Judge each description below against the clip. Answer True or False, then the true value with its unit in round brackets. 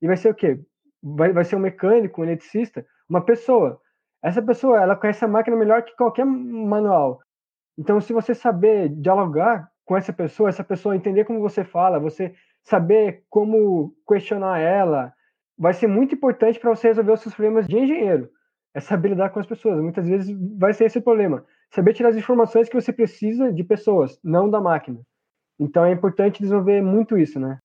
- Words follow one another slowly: False (185 wpm)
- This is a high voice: True (210 Hz)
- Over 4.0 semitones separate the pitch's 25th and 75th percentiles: False (3.4 semitones)